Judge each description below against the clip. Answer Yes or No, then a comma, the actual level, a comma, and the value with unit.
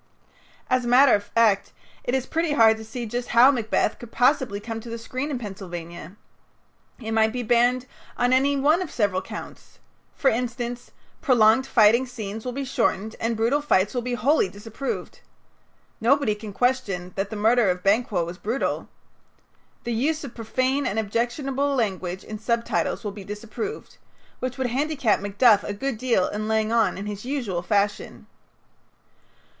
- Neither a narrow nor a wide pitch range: Yes, average, 3.6 semitones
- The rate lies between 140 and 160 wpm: No, average, 170 wpm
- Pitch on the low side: No, high, 230 Hz